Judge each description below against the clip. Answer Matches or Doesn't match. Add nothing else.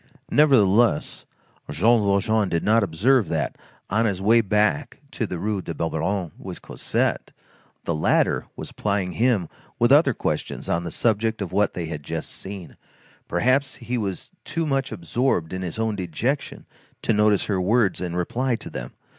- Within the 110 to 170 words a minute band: Matches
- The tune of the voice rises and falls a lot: Doesn't match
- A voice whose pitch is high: Doesn't match